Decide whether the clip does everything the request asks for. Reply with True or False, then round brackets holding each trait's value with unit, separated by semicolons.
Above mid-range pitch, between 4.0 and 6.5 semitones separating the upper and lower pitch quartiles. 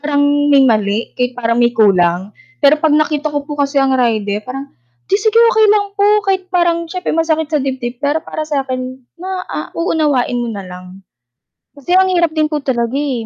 True (285 Hz; 5.2 semitones)